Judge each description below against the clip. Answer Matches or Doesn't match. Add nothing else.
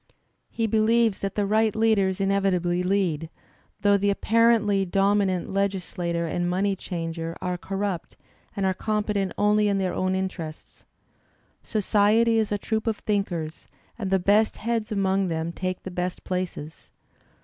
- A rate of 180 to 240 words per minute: Doesn't match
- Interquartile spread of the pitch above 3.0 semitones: Doesn't match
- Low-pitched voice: Doesn't match